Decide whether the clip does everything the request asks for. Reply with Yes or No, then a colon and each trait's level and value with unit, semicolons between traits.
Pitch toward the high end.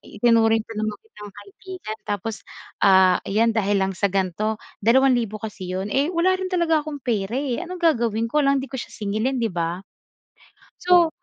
Yes: high, 225 Hz